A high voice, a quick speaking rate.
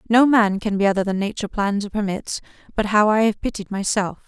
Yes: high, 205 Hz; fast, 225 wpm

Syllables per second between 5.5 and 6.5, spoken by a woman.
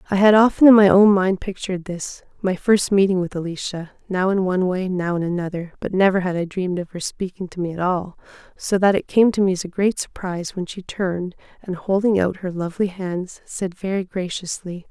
Yes: 5.6 syllables/s; female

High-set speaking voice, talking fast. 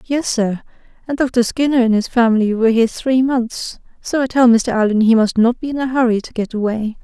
Yes: high, 235 Hz; fast, 220 wpm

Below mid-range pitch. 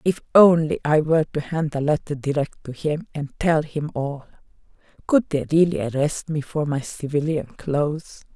No: medium, 150 Hz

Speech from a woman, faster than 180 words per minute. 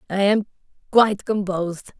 No: female; slow, 90 wpm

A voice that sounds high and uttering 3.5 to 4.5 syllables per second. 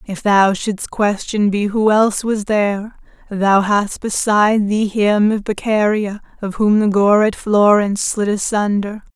Yes: high, 205 Hz; 4.3 syllables/s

